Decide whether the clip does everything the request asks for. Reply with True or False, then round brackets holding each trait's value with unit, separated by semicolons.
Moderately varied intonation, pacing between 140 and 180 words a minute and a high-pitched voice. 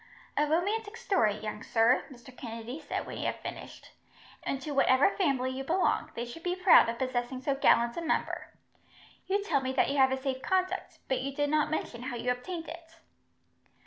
False (4.8 semitones; 200 wpm; 270 Hz)